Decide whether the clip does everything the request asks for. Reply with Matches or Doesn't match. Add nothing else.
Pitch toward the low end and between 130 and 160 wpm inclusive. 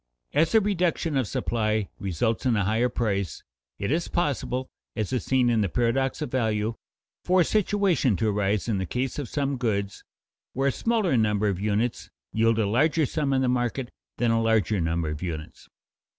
Doesn't match